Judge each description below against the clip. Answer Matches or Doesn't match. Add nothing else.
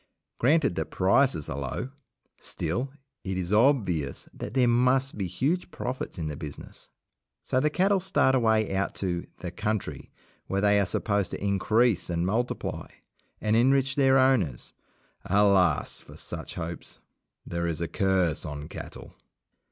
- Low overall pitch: Matches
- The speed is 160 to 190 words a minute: Doesn't match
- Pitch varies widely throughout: Matches